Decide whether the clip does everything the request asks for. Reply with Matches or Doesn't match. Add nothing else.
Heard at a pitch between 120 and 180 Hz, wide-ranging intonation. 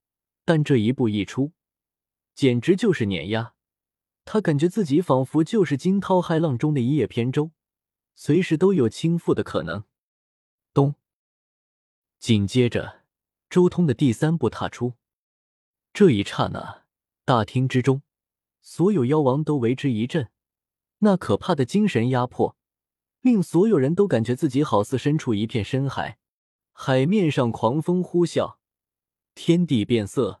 Matches